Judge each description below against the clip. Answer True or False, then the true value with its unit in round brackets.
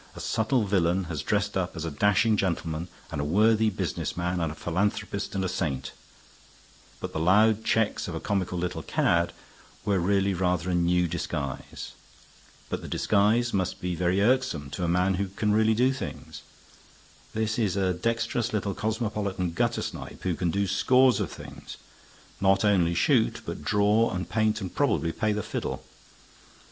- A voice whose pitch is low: True (95 Hz)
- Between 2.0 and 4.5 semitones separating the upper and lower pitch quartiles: True (3.5 semitones)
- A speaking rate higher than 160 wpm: True (170 wpm)